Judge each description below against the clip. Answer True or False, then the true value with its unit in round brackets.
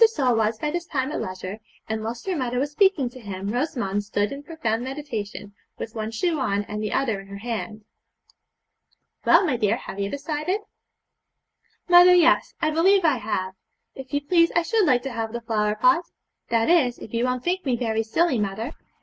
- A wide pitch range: True (6.3 semitones)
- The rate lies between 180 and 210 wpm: True (200 wpm)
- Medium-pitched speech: False (245 Hz)